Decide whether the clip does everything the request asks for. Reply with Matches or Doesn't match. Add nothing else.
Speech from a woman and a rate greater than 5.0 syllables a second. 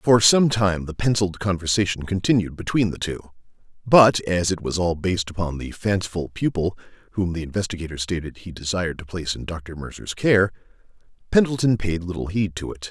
Doesn't match